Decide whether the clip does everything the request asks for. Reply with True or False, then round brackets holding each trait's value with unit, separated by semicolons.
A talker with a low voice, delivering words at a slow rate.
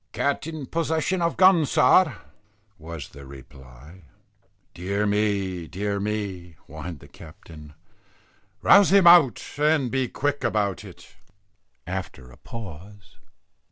True (100 Hz; 120 wpm)